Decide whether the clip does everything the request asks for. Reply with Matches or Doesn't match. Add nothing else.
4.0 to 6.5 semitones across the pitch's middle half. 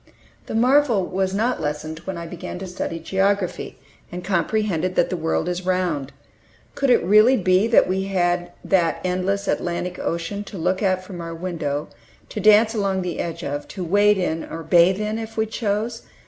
Doesn't match